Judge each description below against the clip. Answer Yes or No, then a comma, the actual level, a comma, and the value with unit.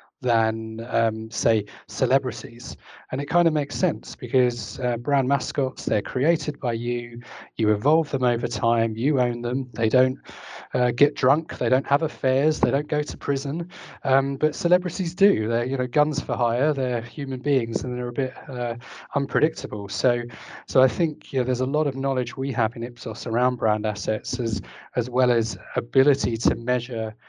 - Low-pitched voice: Yes, low, 125 Hz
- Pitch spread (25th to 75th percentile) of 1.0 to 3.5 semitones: Yes, average, 3.1 semitones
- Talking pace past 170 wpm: Yes, average, 185 wpm